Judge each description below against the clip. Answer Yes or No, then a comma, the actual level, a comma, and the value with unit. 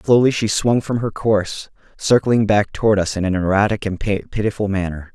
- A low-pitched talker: Yes, low, 105 Hz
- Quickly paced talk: No, average, 185 wpm